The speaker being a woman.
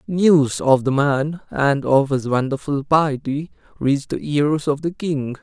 No: male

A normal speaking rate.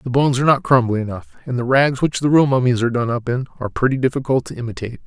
No: fast, 260 wpm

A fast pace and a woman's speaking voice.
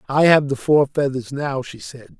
No: fast, 220 wpm; male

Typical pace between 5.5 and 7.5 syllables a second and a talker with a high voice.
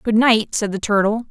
No: 5.0 syllables/s; high, 215 Hz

